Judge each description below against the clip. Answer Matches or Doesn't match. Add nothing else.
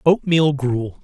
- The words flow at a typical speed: Matches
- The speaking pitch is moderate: Matches